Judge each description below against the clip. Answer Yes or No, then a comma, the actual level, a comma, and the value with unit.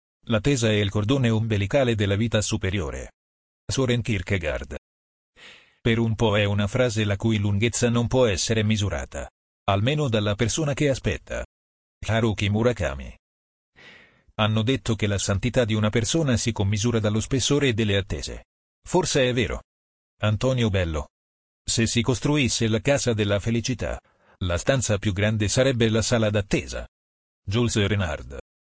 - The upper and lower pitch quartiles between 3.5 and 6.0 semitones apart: Yes, wide, 5.5 semitones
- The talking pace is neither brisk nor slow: Yes, average, 140 wpm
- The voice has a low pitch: Yes, low, 105 Hz